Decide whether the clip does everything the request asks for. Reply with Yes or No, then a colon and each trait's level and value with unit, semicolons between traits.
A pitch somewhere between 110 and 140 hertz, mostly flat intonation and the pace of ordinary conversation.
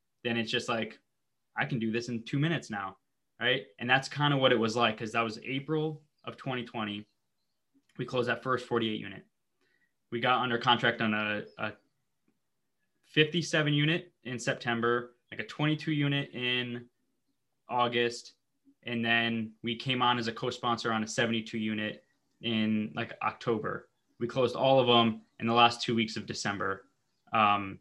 Yes: low, 120 Hz; narrow, 2.3 semitones; average, 170 wpm